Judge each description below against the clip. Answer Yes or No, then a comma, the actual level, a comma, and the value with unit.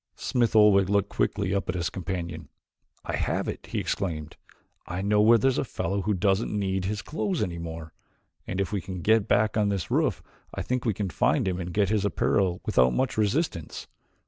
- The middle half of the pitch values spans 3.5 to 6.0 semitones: No, average, 3.1 semitones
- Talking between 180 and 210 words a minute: Yes, average, 200 wpm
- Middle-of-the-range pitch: No, low, 100 Hz